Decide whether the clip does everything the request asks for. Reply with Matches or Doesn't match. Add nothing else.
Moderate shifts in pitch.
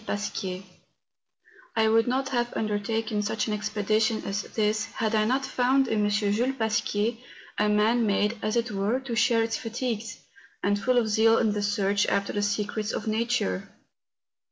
Doesn't match